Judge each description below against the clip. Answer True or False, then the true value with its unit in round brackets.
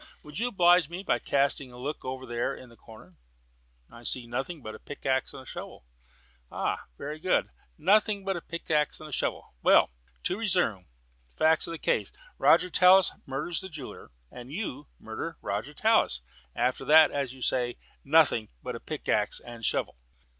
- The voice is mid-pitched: True (145 Hz)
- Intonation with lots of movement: True (6.0 semitones)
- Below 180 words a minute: True (170 wpm)